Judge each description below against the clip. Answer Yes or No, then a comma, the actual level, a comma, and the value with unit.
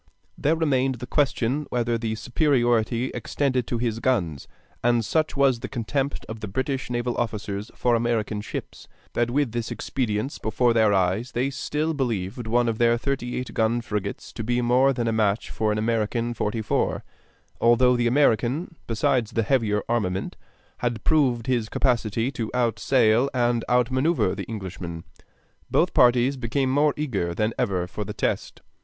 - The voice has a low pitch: Yes, low, 120 Hz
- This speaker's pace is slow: No, average, 165 wpm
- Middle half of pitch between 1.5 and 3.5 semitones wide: Yes, average, 2.8 semitones